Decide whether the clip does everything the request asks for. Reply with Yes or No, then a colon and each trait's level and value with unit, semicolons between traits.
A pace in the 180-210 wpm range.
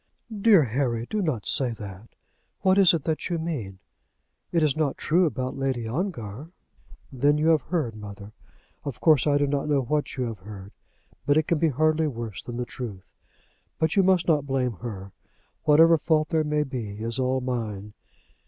Yes: average, 185 wpm